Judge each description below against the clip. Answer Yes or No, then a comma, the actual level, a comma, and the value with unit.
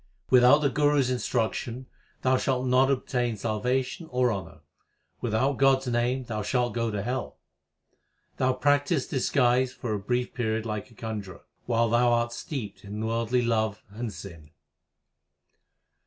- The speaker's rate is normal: Yes, average, 150 wpm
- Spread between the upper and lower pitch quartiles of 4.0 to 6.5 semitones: No, average, 2.8 semitones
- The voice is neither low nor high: No, low, 120 Hz